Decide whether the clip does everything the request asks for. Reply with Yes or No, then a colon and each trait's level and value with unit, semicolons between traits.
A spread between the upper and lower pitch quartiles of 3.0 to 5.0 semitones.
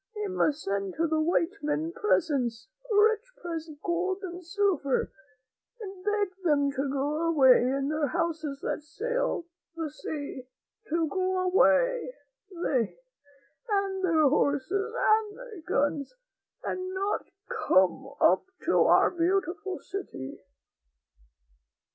No: wide, 5.4 semitones